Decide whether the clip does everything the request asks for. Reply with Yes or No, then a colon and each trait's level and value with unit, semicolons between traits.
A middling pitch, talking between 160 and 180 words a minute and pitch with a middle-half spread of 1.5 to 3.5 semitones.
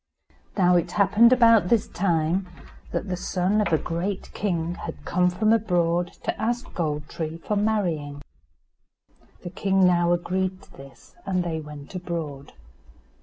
No: medium, 180 Hz; average, 150 wpm; average, 3.2 semitones